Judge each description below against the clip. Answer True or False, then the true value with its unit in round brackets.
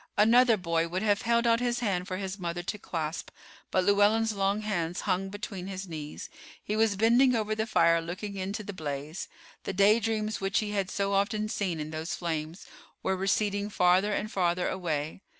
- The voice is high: True (195 Hz)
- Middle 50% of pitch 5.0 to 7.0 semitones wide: False (3.3 semitones)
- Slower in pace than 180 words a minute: False (185 wpm)